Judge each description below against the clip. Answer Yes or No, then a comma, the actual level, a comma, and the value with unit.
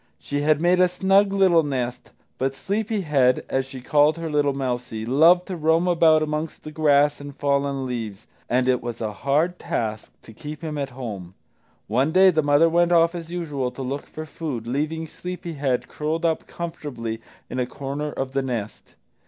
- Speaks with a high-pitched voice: No, medium, 145 Hz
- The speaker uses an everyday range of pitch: Yes, average, 4.3 semitones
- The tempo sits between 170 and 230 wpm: Yes, average, 190 wpm